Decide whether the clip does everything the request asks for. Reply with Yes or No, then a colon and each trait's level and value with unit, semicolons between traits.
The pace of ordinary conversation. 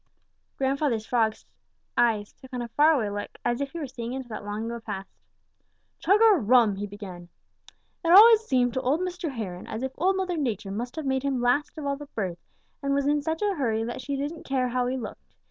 No: fast, 225 wpm